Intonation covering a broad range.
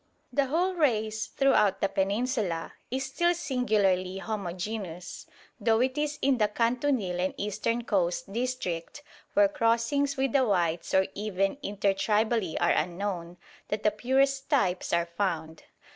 Yes: wide, 5.8 semitones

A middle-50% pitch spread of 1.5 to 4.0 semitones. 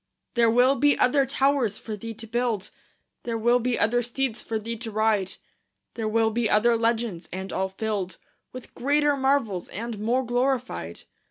Yes: narrow, 2.6 semitones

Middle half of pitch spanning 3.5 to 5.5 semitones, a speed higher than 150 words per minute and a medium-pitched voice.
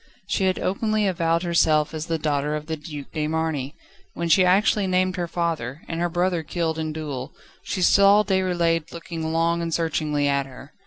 No: average, 2.9 semitones; average, 190 wpm; medium, 165 Hz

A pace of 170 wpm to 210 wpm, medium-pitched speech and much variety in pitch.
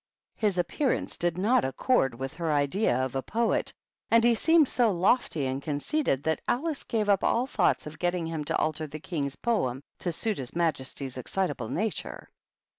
Yes: average, 185 wpm; medium, 170 Hz; wide, 8.0 semitones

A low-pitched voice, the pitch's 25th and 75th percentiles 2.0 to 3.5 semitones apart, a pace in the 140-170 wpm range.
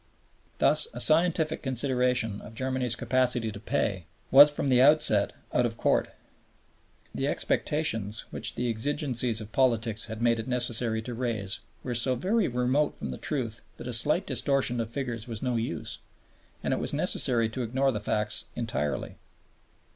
Yes: low, 120 Hz; average, 2.9 semitones; average, 160 wpm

